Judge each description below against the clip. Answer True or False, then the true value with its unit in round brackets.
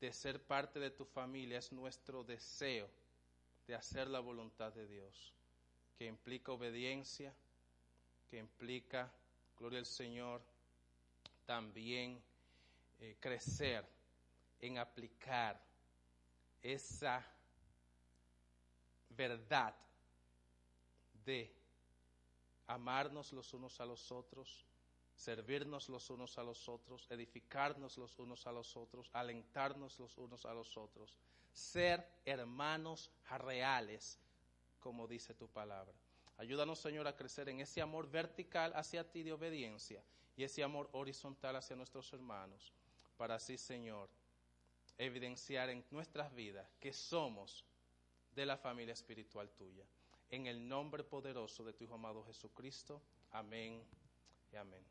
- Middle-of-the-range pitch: False (120 Hz)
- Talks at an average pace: False (115 wpm)